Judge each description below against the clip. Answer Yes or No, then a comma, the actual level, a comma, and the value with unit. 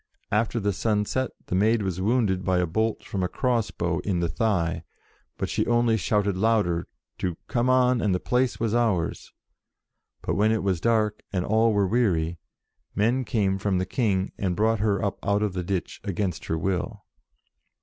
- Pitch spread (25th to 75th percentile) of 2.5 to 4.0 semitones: Yes, average, 3.5 semitones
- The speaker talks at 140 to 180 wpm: No, average, 190 wpm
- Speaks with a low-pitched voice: Yes, low, 100 Hz